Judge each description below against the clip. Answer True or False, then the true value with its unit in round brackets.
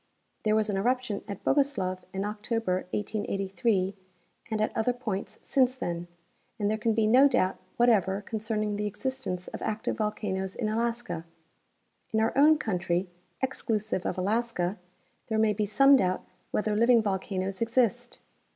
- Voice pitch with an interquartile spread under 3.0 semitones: False (3.4 semitones)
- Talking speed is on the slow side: False (150 wpm)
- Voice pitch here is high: True (215 Hz)